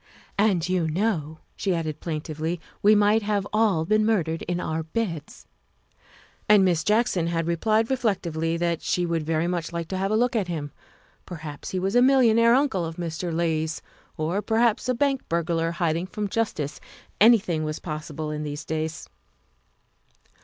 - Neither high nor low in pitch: Yes, medium, 175 Hz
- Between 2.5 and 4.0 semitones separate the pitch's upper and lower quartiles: No, average, 4.8 semitones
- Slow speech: No, average, 175 wpm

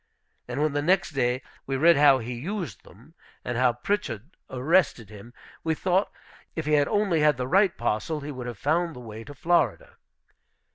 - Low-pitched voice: No, medium, 145 Hz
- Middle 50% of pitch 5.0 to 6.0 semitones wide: Yes, wide, 5.4 semitones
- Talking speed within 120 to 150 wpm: No, average, 190 wpm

